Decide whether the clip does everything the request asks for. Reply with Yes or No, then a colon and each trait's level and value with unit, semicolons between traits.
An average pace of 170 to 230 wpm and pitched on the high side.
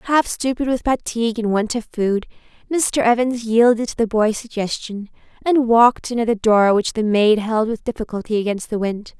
Yes: average, 195 wpm; high, 225 Hz